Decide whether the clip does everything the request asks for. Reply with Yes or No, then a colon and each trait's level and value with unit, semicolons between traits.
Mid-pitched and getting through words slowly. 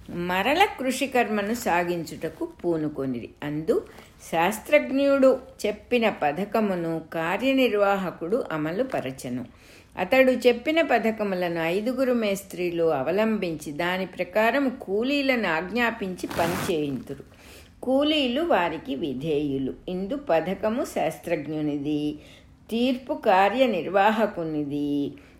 No: high, 195 Hz; slow, 70 wpm